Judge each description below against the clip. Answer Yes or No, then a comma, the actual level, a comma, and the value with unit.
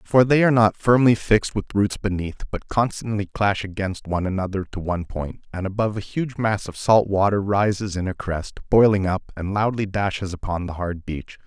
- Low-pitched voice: Yes, low, 100 Hz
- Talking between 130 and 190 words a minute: No, fast, 205 wpm